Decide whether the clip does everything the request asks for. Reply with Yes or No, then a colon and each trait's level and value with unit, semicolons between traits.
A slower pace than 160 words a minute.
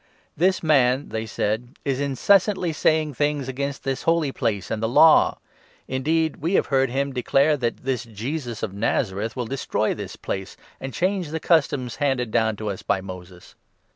No: average, 175 wpm